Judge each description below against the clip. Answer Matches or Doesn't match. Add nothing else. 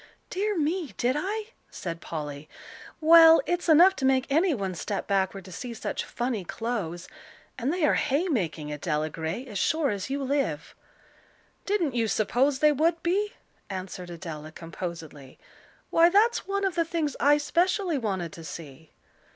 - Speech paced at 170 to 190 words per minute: Doesn't match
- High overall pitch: Matches